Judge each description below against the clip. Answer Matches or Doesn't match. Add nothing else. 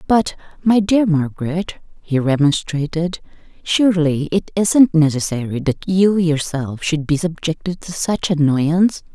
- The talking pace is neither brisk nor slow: Doesn't match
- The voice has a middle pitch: Matches